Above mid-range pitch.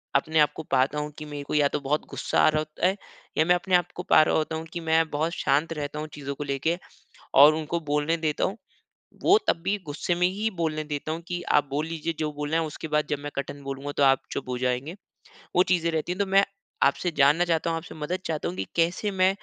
No: medium, 155 Hz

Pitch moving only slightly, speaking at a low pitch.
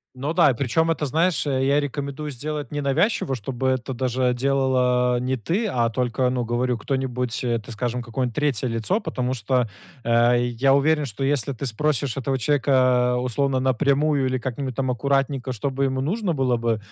Yes: narrow, 2.2 semitones; low, 130 Hz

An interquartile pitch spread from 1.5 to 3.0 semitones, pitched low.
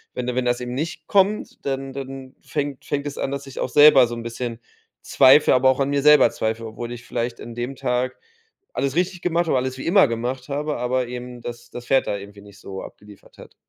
Yes: average, 2.7 semitones; low, 130 Hz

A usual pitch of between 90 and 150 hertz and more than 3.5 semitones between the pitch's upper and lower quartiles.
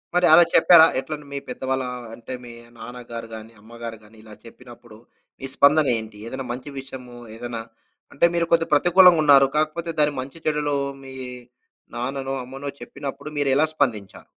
Yes: low, 135 Hz; average, 3.9 semitones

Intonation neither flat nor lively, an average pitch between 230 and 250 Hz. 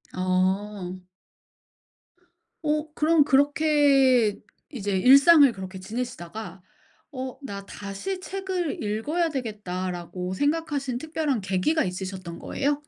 No: wide, 7.8 semitones; high, 245 Hz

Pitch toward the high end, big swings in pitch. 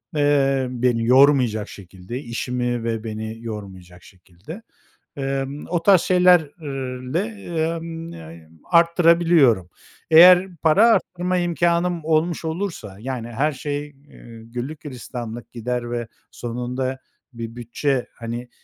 No: low, 130 Hz; wide, 5.8 semitones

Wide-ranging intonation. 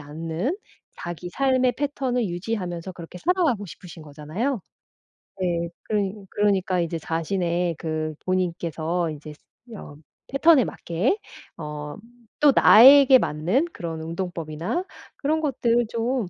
Yes: wide, 7.1 semitones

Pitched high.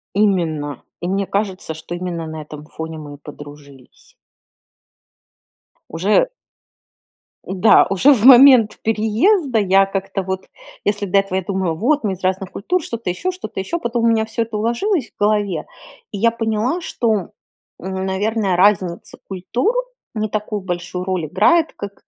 Yes: high, 195 Hz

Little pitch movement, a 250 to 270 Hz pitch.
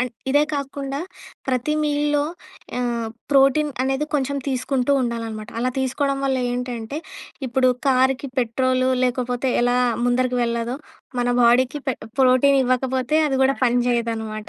Yes: narrow, 2.0 semitones; very high, 255 Hz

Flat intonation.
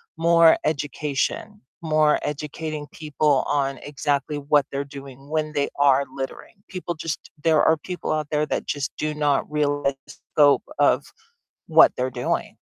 Yes: narrow, 1.6 semitones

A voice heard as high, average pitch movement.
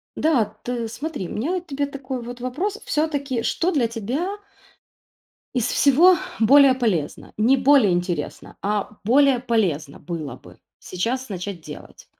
No: high, 245 Hz; wide, 5.7 semitones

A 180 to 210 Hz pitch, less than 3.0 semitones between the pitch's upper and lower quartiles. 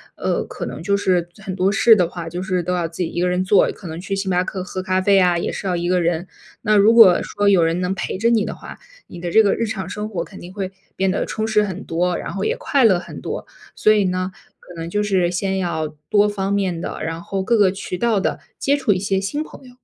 Yes: high, 190 Hz; narrow, 2.4 semitones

